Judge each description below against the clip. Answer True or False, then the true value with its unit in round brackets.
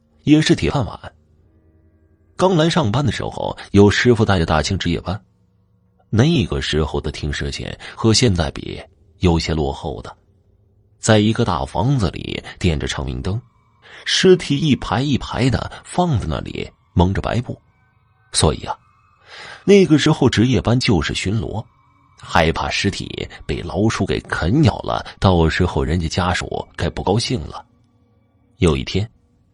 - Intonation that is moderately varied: False (6.3 semitones)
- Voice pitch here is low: True (100 Hz)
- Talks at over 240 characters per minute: False (215 characters per minute)